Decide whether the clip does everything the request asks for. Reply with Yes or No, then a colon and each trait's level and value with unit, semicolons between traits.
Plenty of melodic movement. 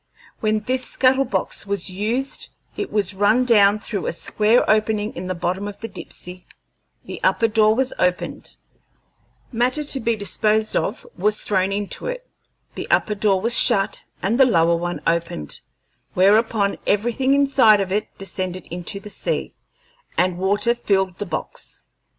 No: average, 3.5 semitones